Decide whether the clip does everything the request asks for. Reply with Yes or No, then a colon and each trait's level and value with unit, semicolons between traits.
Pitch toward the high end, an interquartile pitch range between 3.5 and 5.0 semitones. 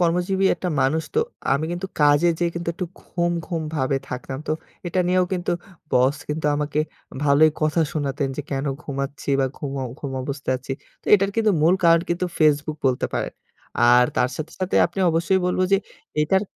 No: medium, 155 Hz; average, 3.9 semitones